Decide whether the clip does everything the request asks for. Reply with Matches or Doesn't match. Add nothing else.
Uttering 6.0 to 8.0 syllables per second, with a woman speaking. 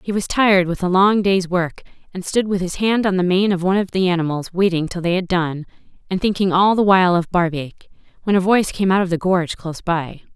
Matches